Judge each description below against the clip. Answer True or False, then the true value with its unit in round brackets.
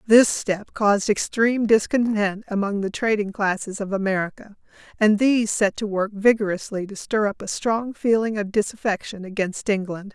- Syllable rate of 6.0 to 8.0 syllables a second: False (5.0 syllables/s)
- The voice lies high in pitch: True (210 Hz)